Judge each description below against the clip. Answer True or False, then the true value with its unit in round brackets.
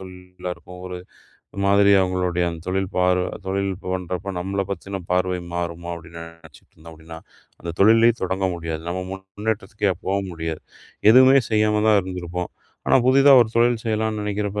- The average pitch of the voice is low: True (95 Hz)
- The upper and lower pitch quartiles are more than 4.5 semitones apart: False (2.8 semitones)